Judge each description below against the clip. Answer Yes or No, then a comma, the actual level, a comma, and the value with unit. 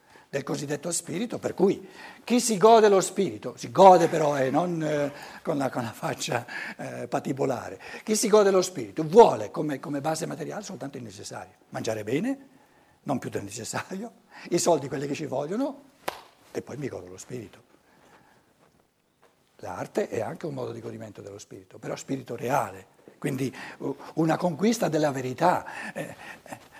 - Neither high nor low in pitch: Yes, medium, 165 Hz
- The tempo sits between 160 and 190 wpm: Yes, average, 165 wpm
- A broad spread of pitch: Yes, wide, 6.9 semitones